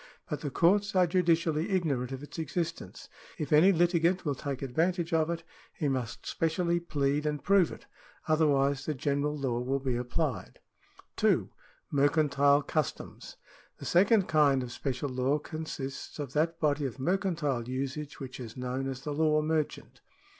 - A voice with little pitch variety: No, average, 3.4 semitones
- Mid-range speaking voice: Yes, medium, 150 Hz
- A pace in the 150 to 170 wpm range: Yes, average, 160 wpm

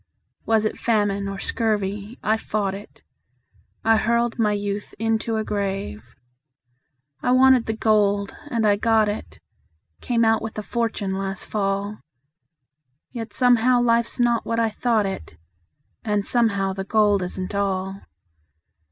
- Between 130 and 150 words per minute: Yes, average, 140 wpm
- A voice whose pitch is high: Yes, high, 215 Hz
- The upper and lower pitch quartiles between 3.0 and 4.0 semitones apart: No, narrow, 2.4 semitones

